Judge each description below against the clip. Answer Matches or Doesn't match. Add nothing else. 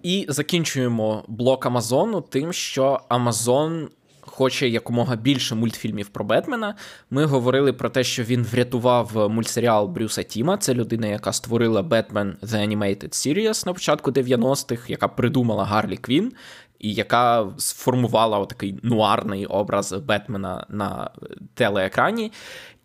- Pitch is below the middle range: Matches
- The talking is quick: Doesn't match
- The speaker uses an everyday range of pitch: Matches